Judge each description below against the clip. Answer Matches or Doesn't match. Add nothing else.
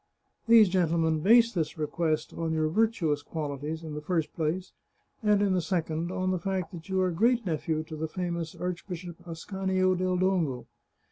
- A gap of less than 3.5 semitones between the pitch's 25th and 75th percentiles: Matches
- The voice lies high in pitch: Doesn't match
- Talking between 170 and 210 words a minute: Matches